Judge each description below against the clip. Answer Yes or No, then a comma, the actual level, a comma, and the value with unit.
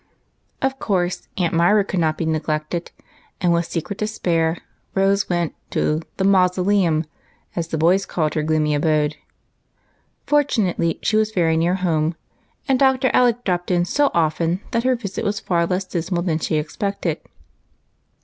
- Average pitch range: Yes, average, 3.6 semitones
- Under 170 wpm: Yes, average, 160 wpm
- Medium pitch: Yes, medium, 175 Hz